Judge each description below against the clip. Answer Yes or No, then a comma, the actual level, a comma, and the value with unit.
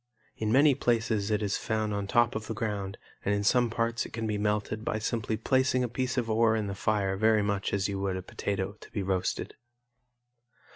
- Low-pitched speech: Yes, low, 110 Hz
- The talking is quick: Yes, fast, 215 wpm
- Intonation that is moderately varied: No, narrow, 2.3 semitones